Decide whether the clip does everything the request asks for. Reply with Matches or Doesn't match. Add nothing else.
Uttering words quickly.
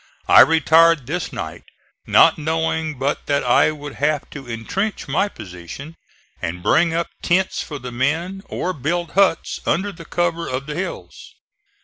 Doesn't match